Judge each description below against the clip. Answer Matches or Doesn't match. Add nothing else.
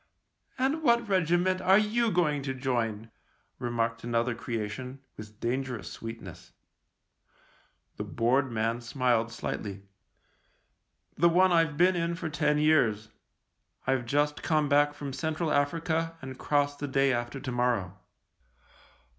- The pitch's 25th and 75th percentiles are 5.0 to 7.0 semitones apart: Matches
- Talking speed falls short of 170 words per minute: Matches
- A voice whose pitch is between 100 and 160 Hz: Matches